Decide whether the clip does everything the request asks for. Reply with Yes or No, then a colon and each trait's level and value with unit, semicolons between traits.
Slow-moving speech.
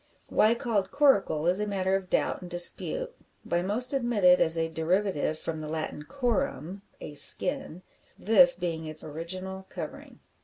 No: average, 155 wpm